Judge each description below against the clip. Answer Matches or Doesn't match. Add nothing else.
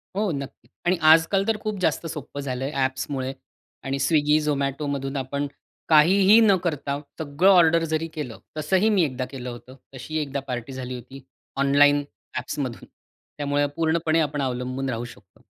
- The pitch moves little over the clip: Doesn't match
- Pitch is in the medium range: Matches